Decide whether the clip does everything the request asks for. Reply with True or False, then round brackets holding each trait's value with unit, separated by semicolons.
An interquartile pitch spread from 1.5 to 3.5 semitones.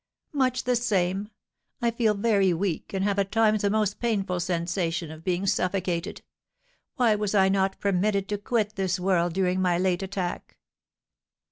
True (2.6 semitones)